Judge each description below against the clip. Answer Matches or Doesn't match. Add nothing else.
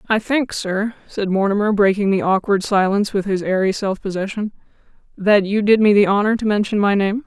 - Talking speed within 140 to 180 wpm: Doesn't match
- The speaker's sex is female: Matches